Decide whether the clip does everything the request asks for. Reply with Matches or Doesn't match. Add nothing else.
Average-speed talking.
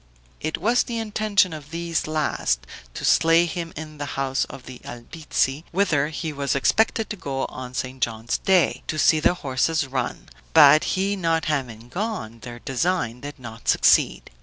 Matches